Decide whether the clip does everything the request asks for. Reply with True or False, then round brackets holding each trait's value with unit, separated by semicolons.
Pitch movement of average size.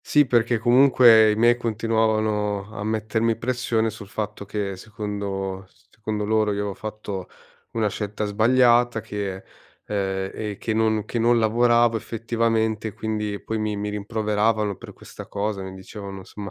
False (1.8 semitones)